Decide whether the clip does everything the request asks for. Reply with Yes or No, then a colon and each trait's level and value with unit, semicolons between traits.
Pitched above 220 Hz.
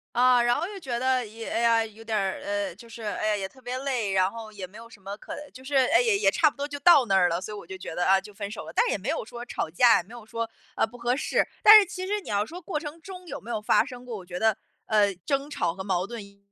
Yes: high, 230 Hz